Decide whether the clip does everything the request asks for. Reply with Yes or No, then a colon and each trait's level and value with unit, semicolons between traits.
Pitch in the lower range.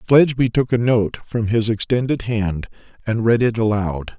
Yes: low, 115 Hz